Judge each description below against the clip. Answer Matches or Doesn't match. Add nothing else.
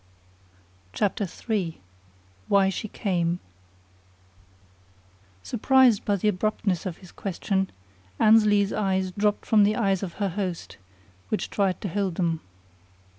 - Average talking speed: Doesn't match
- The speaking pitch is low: Doesn't match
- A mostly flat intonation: Matches